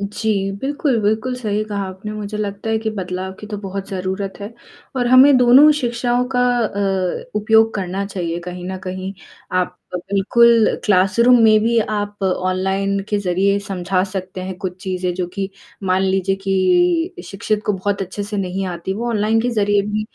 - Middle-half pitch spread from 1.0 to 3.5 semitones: Yes, average, 2.7 semitones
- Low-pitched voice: No, high, 200 Hz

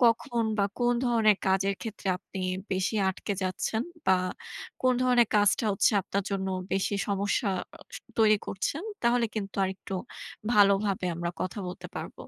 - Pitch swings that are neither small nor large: Yes, average, 3.2 semitones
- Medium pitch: No, high, 205 Hz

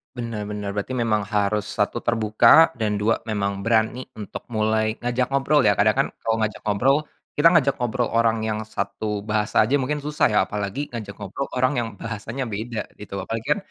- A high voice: No, low, 110 Hz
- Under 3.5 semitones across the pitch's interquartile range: Yes, average, 2.8 semitones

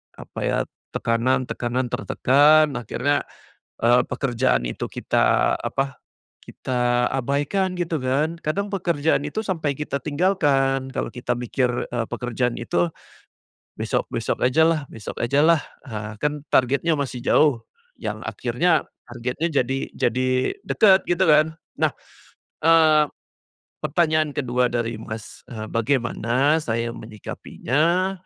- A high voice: No, low, 135 Hz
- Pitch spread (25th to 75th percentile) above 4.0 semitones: Yes, average, 4.4 semitones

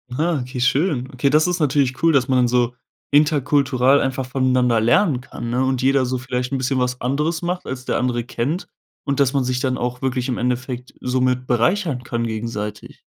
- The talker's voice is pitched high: No, low, 130 Hz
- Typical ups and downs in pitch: No, narrow, 2.1 semitones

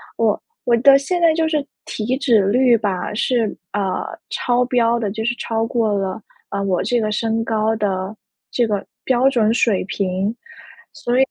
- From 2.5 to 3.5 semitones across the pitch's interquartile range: Yes, average, 3.0 semitones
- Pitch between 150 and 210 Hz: No, high, 225 Hz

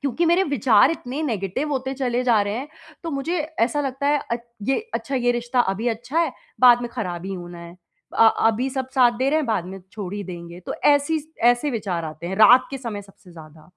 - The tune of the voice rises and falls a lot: Yes, wide, 5.7 semitones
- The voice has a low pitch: No, high, 240 Hz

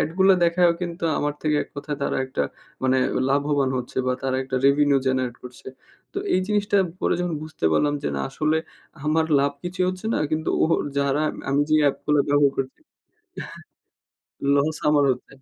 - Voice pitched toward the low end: No, medium, 145 Hz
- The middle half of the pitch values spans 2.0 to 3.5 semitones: Yes, average, 2.9 semitones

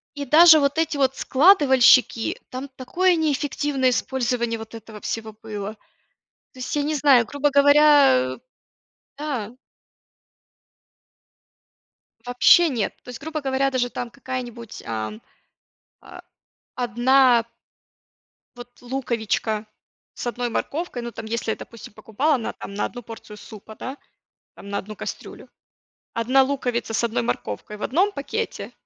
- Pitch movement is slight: No, average, 3.9 semitones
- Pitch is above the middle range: Yes, very high, 250 Hz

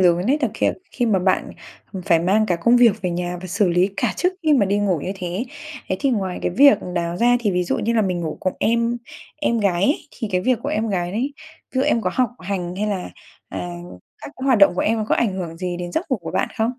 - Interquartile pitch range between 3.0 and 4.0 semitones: No, average, 4.7 semitones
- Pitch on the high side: Yes, high, 200 Hz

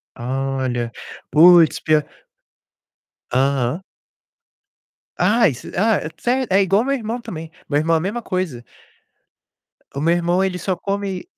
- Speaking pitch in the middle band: Yes, medium, 175 Hz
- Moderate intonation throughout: No, wide, 6.0 semitones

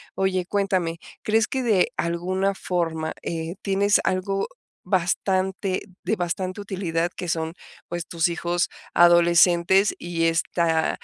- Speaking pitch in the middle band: Yes, medium, 175 Hz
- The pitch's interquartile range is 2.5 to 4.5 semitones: No, narrow, 2.1 semitones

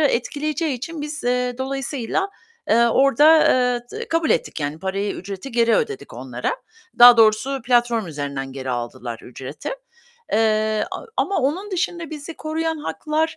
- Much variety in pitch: Yes, wide, 6.6 semitones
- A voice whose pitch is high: Yes, very high, 250 Hz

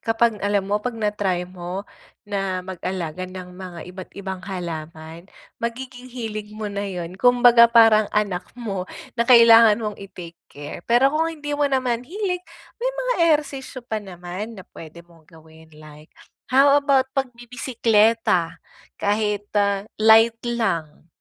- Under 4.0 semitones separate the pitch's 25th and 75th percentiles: No, average, 4.9 semitones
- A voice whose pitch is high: Yes, high, 210 Hz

